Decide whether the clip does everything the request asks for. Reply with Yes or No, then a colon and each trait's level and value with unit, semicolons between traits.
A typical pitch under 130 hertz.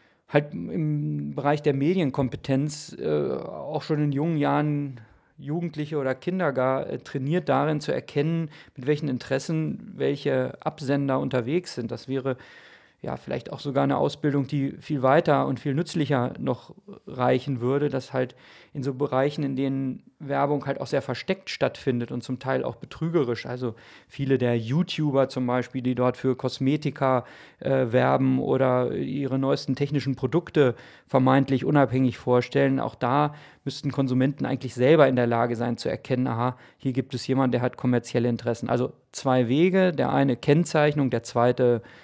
No: low, 135 Hz